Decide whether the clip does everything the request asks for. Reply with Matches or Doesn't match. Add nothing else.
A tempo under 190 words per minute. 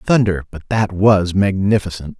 Matches